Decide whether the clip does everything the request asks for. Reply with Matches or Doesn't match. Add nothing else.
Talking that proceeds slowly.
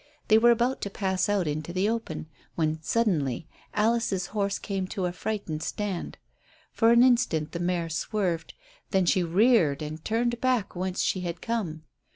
Doesn't match